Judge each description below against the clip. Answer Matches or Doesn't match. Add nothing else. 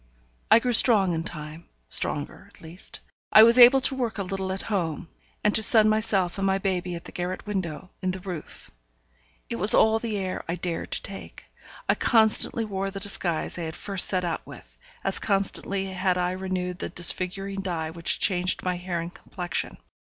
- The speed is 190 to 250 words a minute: Matches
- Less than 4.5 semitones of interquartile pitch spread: Matches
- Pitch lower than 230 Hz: Matches